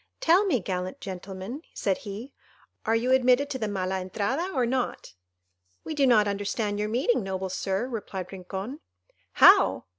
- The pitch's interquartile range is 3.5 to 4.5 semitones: No, average, 5.0 semitones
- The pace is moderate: Yes, average, 155 wpm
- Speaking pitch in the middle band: No, high, 210 Hz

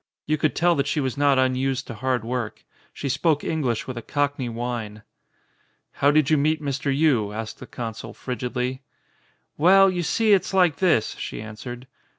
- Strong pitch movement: No, average, 4.1 semitones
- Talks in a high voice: No, low, 135 Hz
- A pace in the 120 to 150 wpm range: No, average, 175 wpm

